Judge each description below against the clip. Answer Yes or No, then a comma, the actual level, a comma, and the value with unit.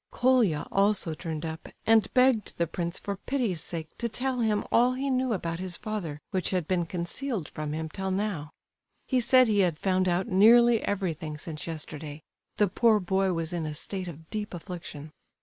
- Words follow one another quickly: No, average, 185 wpm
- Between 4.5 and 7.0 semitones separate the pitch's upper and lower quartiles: Yes, average, 5.1 semitones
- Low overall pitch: No, medium, 185 Hz